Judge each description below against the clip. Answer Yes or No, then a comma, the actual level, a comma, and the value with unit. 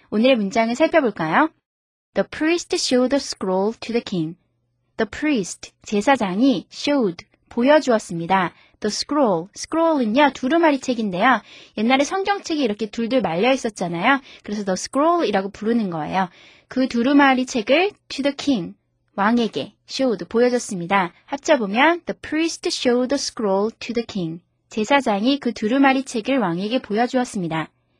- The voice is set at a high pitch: Yes, high, 240 Hz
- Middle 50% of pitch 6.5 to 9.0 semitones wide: No, average, 5.3 semitones